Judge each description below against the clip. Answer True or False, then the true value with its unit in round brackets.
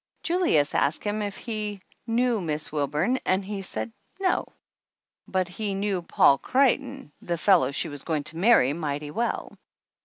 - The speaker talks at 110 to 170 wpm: True (155 wpm)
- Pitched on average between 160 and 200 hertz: True (190 Hz)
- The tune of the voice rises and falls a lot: True (6.9 semitones)